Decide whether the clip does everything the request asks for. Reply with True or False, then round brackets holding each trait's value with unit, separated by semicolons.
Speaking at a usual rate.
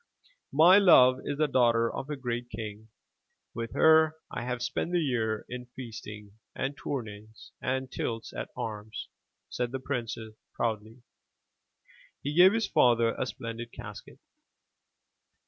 True (145 wpm)